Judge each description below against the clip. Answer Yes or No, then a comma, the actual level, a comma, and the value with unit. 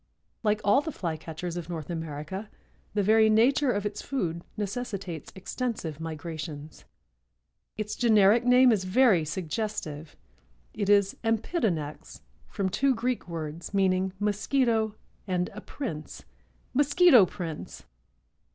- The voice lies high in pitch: Yes, high, 200 Hz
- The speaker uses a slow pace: Yes, slow, 115 wpm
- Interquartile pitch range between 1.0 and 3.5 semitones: No, average, 5.2 semitones